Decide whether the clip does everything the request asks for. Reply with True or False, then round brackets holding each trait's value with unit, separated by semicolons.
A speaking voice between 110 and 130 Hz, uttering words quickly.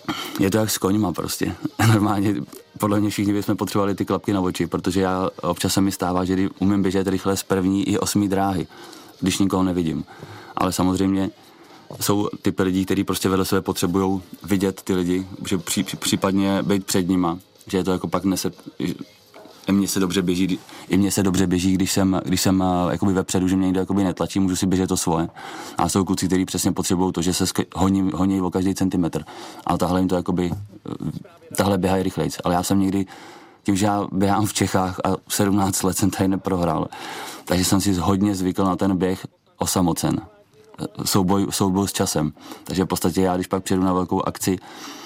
False (95 Hz; 195 wpm)